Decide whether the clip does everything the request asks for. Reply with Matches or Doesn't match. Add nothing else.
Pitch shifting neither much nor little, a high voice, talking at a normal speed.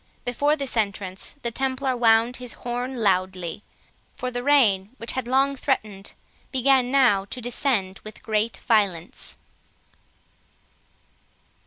Doesn't match